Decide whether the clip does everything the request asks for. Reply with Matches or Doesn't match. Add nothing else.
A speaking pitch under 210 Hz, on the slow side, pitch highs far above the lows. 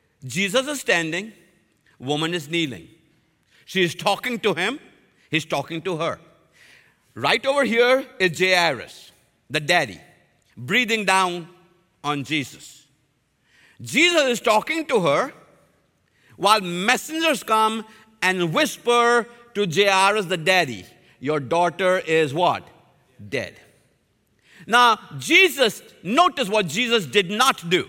Matches